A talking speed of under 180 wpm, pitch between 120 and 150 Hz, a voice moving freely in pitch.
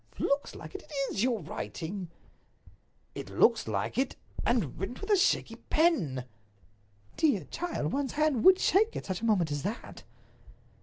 No: average, 160 wpm; very high, 250 Hz; wide, 8.9 semitones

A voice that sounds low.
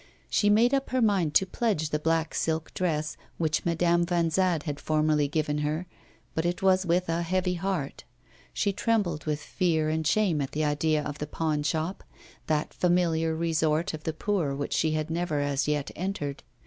No: medium, 160 Hz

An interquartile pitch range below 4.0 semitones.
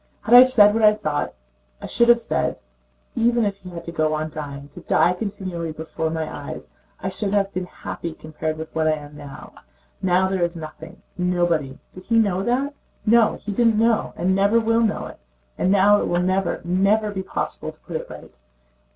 No: average, 4.8 semitones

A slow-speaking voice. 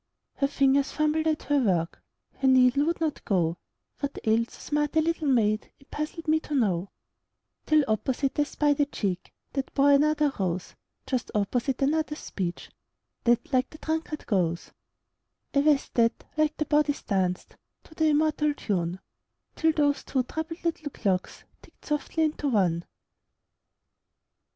No: average, 155 wpm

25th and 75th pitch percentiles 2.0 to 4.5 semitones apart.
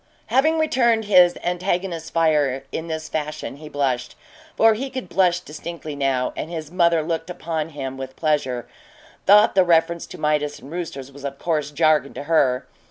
Yes: average, 3.7 semitones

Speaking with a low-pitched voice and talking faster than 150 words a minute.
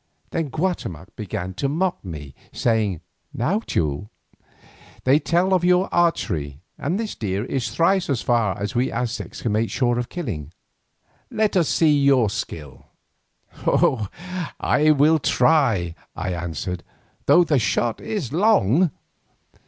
No: low, 125 Hz; slow, 135 wpm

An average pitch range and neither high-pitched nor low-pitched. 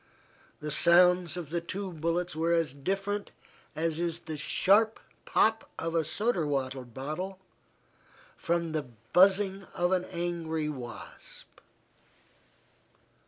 Yes: average, 3.3 semitones; medium, 170 Hz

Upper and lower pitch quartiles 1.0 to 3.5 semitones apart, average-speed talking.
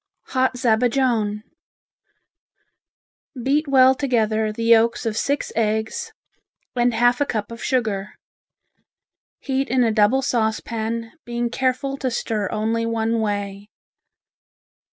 No: average, 2.7 semitones; slow, 110 wpm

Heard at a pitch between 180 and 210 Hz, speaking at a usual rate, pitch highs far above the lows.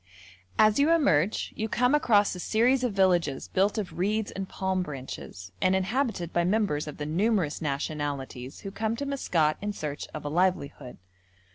Yes: medium, 185 Hz; average, 170 wpm; wide, 6.2 semitones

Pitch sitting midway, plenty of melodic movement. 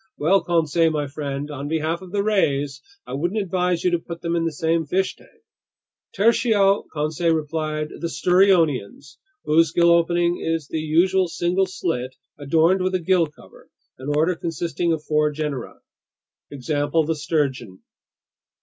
No: medium, 165 Hz; average, 2.9 semitones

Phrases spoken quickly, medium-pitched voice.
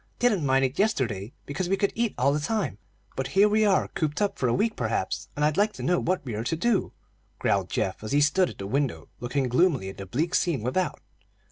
Yes: fast, 240 wpm; medium, 150 Hz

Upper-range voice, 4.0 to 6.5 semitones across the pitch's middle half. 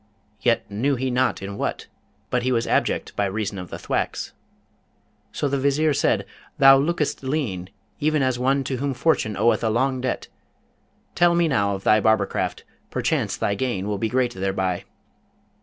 No: low, 125 Hz; average, 5.2 semitones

